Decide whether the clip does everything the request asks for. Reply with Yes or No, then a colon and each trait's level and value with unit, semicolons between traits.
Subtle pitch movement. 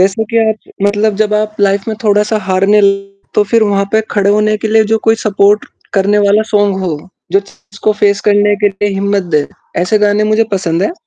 Yes: narrow, 1.3 semitones